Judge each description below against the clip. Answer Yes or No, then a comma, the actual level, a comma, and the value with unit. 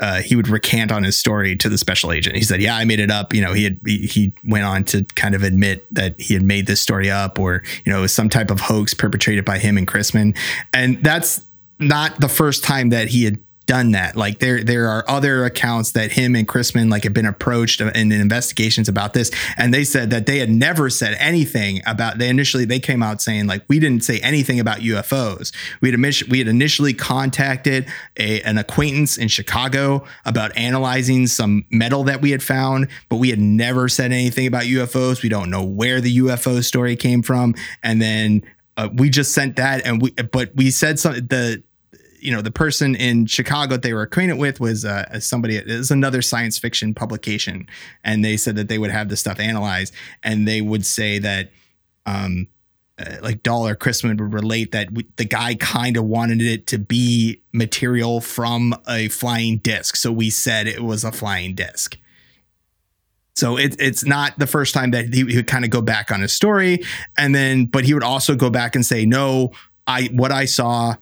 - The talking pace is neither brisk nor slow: No, fast, 210 wpm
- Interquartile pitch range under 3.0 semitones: No, average, 3.3 semitones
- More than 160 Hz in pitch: No, low, 115 Hz